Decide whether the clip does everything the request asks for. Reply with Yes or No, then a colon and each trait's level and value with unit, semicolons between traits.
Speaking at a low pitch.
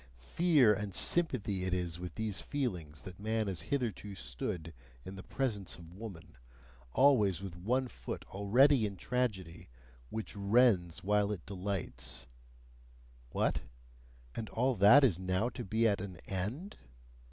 Yes: low, 100 Hz